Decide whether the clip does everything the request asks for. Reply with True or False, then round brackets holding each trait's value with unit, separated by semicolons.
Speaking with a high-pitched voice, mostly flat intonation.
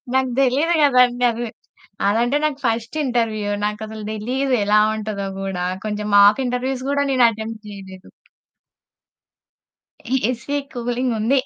False (235 Hz; 3.4 semitones)